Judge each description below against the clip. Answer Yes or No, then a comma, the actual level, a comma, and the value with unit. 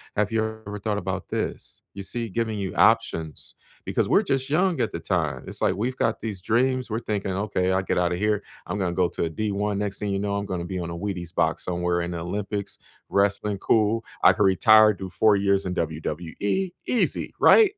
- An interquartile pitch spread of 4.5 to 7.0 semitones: No, average, 3.0 semitones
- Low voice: Yes, low, 100 Hz